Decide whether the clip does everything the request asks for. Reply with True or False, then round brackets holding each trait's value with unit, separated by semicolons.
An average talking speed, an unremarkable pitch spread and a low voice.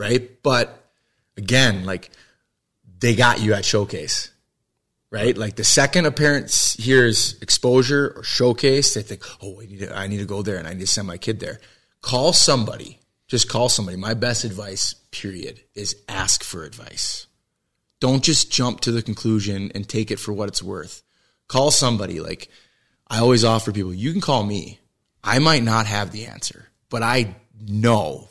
True (180 wpm; 3.5 semitones; 115 Hz)